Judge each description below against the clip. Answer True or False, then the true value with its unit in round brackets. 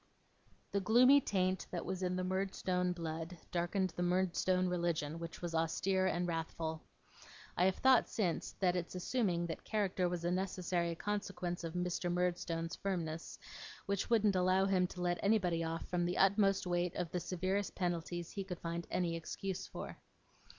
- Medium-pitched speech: True (180 Hz)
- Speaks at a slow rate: False (165 wpm)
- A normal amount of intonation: False (1.7 semitones)